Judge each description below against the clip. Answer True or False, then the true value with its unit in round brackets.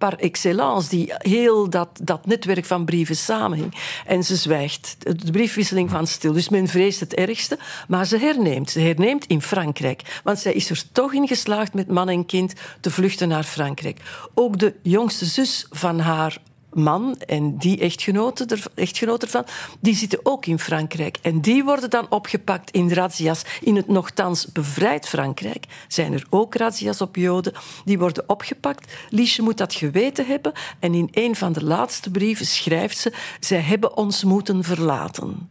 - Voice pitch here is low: False (185 Hz)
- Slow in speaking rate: False (170 wpm)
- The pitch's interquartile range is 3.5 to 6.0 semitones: True (4.4 semitones)